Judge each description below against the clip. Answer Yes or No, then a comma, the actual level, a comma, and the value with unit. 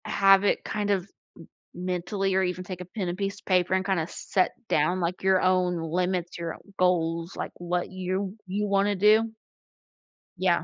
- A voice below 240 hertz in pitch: Yes, medium, 185 Hz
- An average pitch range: No, narrow, 1.6 semitones